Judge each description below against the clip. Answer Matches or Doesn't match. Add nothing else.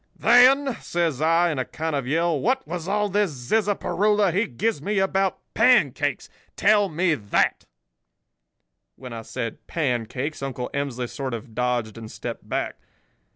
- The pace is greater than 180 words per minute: Doesn't match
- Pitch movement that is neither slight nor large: Doesn't match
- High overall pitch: Doesn't match